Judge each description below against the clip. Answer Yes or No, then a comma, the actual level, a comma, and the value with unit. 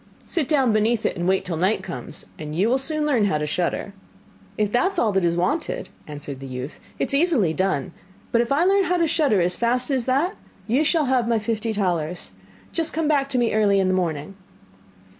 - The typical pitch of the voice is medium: No, high, 225 Hz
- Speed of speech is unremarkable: No, fast, 225 wpm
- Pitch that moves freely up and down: Yes, wide, 7.7 semitones